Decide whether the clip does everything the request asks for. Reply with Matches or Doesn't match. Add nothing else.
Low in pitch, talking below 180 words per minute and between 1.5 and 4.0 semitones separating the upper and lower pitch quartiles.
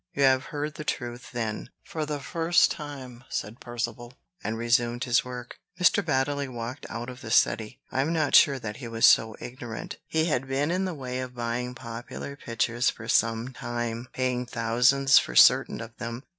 Doesn't match